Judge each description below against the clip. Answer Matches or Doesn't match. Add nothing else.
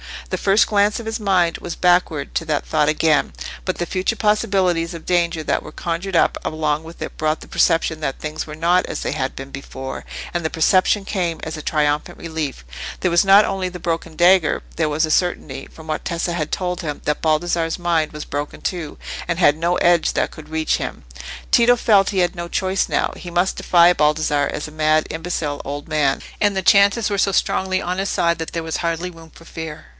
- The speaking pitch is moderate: Matches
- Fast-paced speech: Matches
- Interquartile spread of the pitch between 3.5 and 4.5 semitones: Doesn't match